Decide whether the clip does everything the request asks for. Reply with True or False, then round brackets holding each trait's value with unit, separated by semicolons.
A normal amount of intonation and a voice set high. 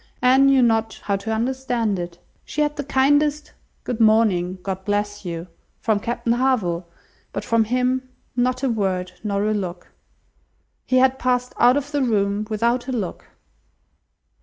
True (4.2 semitones; 230 Hz)